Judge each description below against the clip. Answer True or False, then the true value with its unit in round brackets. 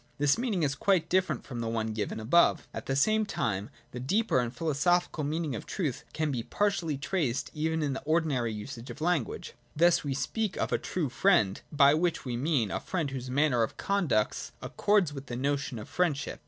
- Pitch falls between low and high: True (145 Hz)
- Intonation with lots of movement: True (5.7 semitones)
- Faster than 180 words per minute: True (200 wpm)